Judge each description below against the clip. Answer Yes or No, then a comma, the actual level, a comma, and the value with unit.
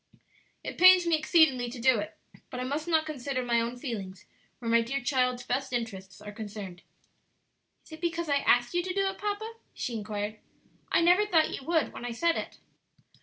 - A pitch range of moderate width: No, wide, 6.3 semitones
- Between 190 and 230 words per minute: Yes, average, 200 wpm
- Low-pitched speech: No, very high, 255 Hz